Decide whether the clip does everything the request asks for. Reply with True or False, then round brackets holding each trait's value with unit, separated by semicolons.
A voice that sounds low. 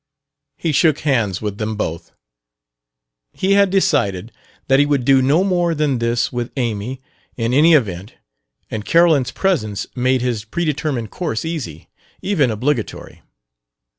True (130 Hz)